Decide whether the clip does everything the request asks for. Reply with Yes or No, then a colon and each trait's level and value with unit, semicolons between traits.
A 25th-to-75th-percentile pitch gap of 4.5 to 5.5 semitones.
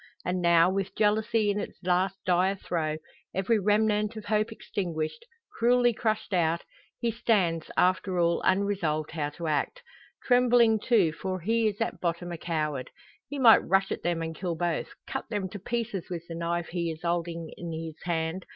No: average, 4.1 semitones